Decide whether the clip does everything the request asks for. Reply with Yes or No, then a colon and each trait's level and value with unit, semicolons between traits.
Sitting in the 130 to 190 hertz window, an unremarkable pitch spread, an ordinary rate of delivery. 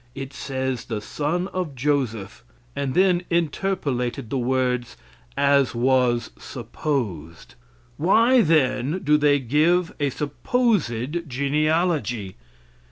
No: medium, 140 Hz; average, 4.7 semitones; slow, 100 wpm